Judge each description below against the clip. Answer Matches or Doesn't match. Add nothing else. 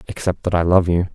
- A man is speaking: Matches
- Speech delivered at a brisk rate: Matches